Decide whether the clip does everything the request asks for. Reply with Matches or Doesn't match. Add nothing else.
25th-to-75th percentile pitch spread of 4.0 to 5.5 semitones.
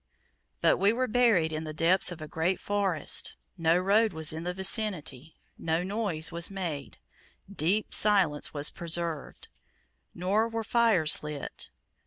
Matches